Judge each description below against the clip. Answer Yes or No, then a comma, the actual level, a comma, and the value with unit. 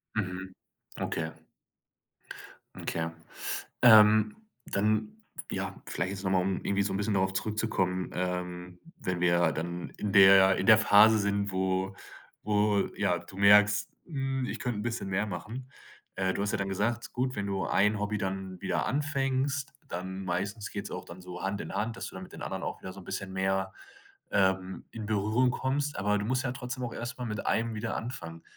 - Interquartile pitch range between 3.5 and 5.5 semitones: No, average, 2.9 semitones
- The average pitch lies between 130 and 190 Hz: No, low, 100 Hz